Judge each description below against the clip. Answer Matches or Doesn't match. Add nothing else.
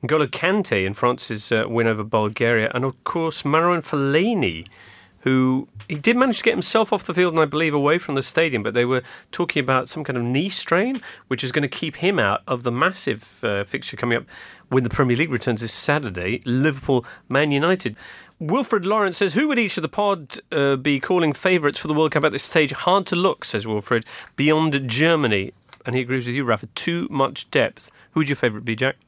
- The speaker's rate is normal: Doesn't match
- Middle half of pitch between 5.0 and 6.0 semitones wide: Matches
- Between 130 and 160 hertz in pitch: Matches